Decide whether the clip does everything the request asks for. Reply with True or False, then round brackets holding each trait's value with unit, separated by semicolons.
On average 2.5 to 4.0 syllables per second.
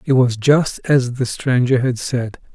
True (3.9 syllables/s)